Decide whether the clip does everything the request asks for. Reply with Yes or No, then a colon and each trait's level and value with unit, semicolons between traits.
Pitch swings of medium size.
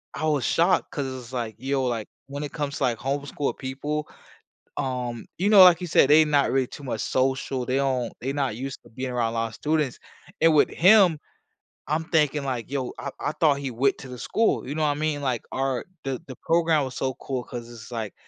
Yes: average, 3.0 semitones